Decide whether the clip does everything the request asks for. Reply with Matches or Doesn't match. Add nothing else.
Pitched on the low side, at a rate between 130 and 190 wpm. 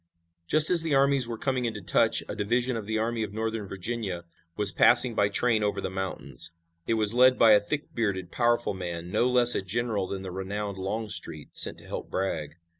Doesn't match